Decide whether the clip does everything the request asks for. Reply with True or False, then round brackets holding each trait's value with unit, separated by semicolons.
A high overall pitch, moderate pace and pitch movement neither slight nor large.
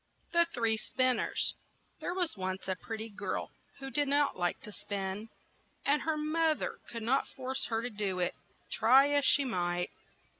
False (240 Hz; 180 wpm; 6.1 semitones)